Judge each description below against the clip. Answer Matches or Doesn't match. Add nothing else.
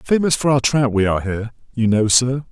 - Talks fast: Matches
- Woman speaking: Doesn't match